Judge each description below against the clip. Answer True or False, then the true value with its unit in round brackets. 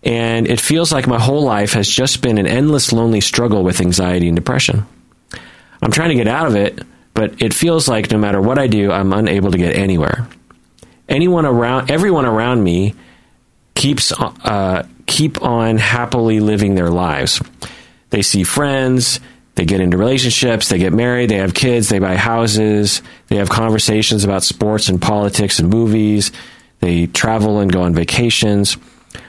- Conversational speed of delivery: True (170 wpm)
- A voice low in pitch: True (110 Hz)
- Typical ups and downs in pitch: True (3.7 semitones)